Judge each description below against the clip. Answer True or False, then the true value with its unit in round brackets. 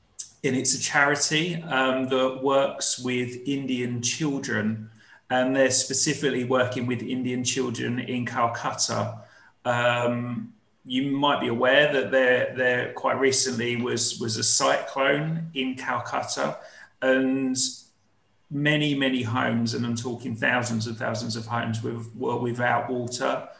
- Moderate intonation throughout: False (2.0 semitones)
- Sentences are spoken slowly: True (130 wpm)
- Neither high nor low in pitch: False (125 Hz)